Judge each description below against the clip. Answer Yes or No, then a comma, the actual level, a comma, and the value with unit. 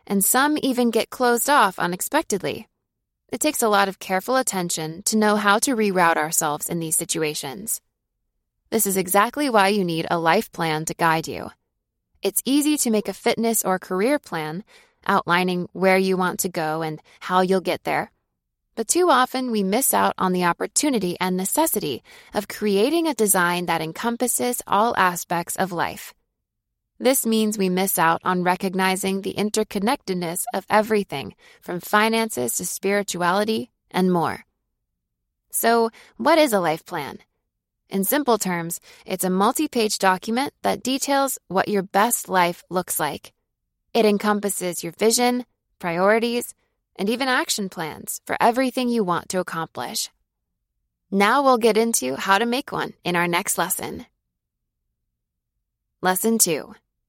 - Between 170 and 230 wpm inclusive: No, average, 150 wpm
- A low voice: No, high, 195 Hz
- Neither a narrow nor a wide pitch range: Yes, average, 4.6 semitones